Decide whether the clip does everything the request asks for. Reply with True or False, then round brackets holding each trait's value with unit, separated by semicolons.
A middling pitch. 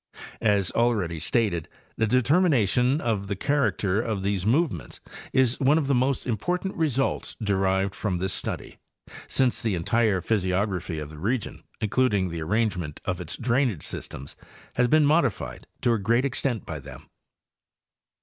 False (110 Hz)